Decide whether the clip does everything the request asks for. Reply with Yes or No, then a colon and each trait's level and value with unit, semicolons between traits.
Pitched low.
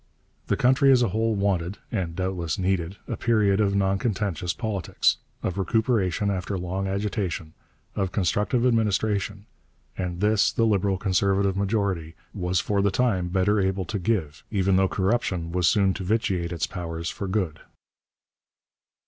Yes: very low, 95 Hz